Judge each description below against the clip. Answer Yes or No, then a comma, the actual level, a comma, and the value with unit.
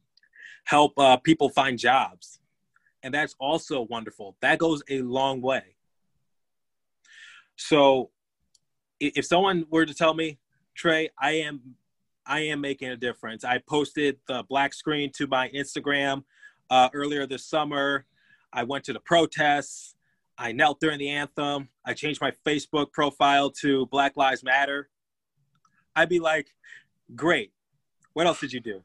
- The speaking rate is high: No, average, 145 wpm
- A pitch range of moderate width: No, narrow, 1.9 semitones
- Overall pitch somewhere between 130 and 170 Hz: Yes, medium, 140 Hz